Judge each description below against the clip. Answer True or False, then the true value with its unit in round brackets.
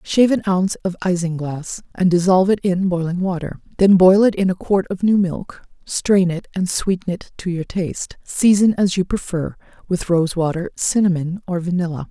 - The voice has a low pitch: False (180 Hz)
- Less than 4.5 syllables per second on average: False (5.1 syllables/s)